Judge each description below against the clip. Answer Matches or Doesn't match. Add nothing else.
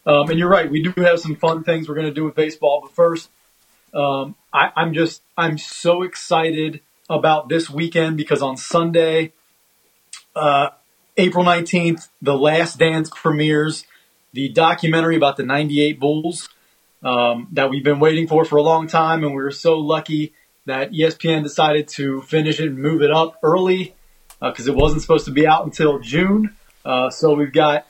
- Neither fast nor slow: Matches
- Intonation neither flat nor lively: Doesn't match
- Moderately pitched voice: Matches